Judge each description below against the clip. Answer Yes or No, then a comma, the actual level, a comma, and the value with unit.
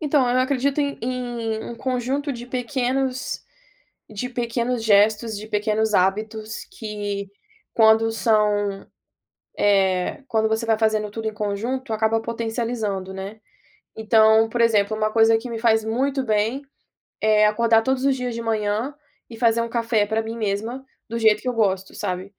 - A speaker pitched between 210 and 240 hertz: Yes, high, 225 Hz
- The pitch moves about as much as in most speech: No, narrow, 2.3 semitones